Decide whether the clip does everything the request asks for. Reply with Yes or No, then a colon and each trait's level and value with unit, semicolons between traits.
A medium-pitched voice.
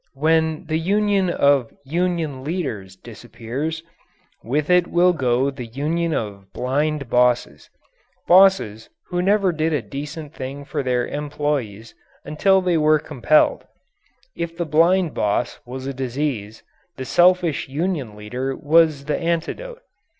Yes: medium, 150 Hz